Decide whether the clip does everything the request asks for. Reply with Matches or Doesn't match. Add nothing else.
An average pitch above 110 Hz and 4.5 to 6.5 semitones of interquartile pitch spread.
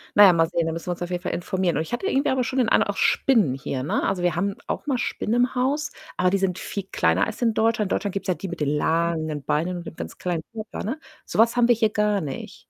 Matches